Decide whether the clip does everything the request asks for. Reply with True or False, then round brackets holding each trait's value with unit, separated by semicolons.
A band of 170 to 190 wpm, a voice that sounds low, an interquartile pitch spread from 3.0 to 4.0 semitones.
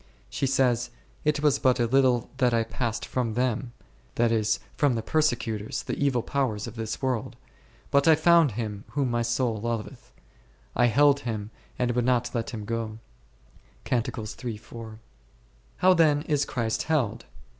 False (155 wpm; 120 Hz; 3.5 semitones)